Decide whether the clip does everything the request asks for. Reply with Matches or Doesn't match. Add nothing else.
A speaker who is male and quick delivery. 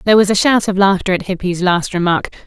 Doesn't match